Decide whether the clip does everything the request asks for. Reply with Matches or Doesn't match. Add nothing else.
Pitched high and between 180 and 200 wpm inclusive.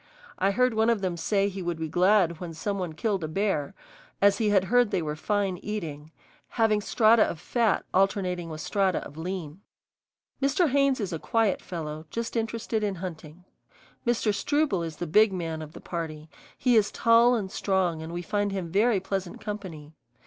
Matches